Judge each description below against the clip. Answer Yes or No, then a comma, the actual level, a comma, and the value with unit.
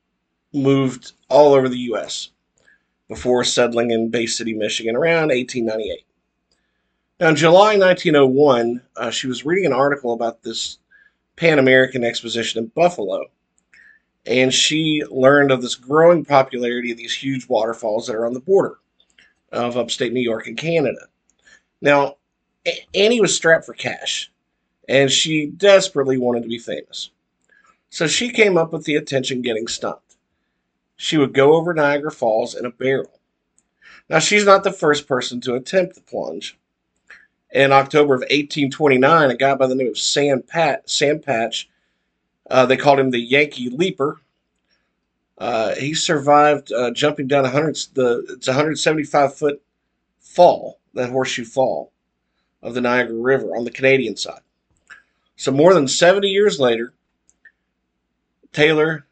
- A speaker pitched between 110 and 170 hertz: Yes, low, 135 Hz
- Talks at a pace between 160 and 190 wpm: No, average, 150 wpm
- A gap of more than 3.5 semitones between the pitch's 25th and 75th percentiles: Yes, average, 4.0 semitones